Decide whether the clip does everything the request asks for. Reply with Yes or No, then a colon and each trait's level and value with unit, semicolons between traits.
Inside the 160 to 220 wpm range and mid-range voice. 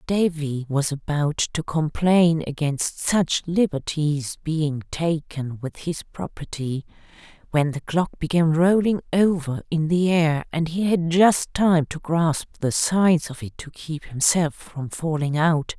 No: average, 150 wpm; medium, 160 Hz